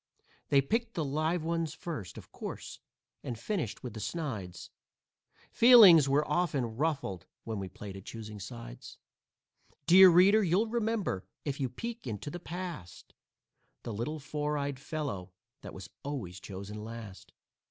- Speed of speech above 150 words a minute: No, average, 145 wpm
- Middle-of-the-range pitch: Yes, medium, 145 Hz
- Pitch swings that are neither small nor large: No, wide, 8.2 semitones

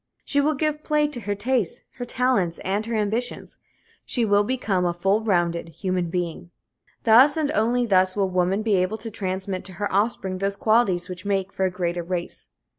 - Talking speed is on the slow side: No, average, 190 wpm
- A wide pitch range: No, average, 4.2 semitones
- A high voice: Yes, high, 200 Hz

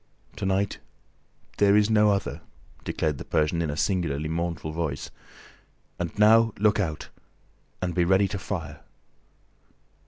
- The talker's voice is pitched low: Yes, very low, 90 Hz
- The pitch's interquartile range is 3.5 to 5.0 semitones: Yes, average, 4.4 semitones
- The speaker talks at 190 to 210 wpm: No, slow, 135 wpm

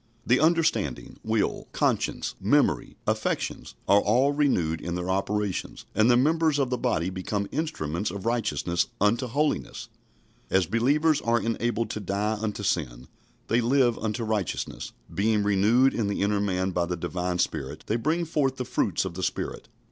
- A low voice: Yes, low, 105 Hz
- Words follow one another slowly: No, average, 165 wpm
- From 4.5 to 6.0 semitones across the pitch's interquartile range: Yes, average, 5.0 semitones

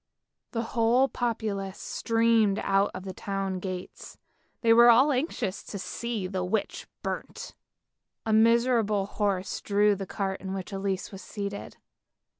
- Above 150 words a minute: No, average, 140 wpm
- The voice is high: Yes, high, 205 Hz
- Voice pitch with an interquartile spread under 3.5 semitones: Yes, average, 2.9 semitones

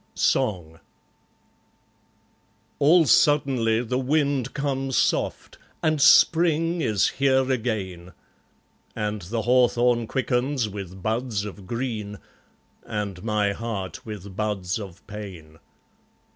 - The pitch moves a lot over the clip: No, average, 4.7 semitones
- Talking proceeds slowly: Yes, slow, 100 wpm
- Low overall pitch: Yes, low, 115 Hz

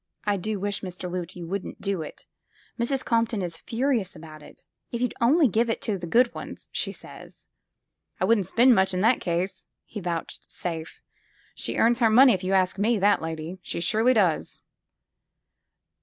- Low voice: No, high, 200 Hz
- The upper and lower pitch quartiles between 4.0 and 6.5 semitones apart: Yes, average, 4.5 semitones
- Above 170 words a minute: Yes, average, 190 wpm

